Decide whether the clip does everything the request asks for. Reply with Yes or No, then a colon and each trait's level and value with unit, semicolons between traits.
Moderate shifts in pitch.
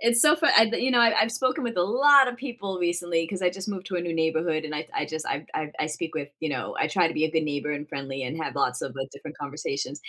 No: wide, 6.8 semitones